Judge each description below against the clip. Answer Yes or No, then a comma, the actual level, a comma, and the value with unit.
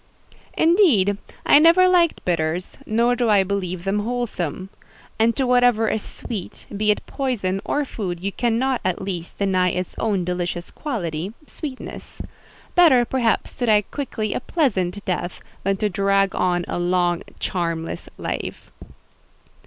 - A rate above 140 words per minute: No, slow, 135 wpm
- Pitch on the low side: No, high, 205 Hz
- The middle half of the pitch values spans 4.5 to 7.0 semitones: Yes, average, 5.2 semitones